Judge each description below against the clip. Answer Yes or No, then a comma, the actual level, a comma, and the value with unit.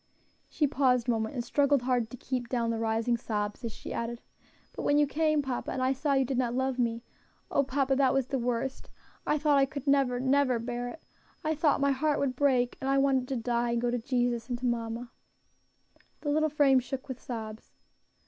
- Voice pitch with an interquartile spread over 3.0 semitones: No, narrow, 2.6 semitones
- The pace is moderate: No, fast, 220 wpm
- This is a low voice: No, very high, 255 Hz